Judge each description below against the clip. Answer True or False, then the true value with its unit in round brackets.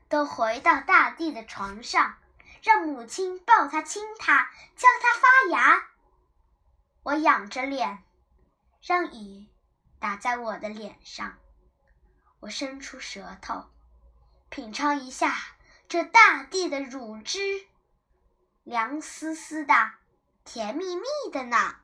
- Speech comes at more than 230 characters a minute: False (150 characters per minute)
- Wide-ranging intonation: True (8.3 semitones)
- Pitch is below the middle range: False (275 Hz)